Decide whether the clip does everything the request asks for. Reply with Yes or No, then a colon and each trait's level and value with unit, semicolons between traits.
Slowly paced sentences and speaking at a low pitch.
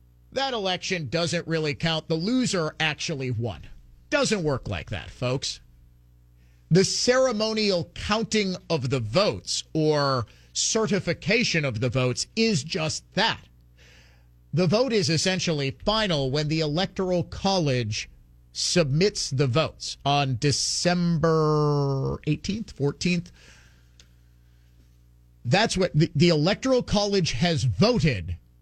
No: slow, 110 wpm; medium, 150 Hz